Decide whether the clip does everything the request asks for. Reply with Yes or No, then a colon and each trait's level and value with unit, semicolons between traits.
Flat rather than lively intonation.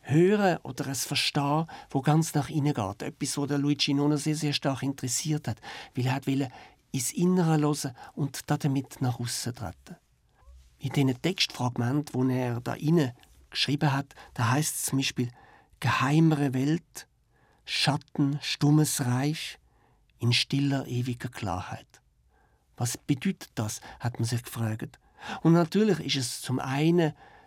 No: average, 3.2 semitones